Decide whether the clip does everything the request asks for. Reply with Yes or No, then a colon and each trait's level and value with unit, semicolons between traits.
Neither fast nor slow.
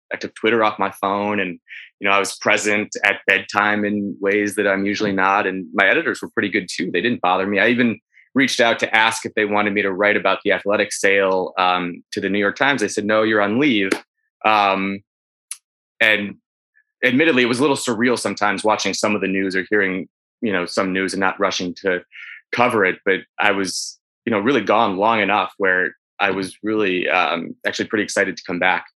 No: fast, 220 wpm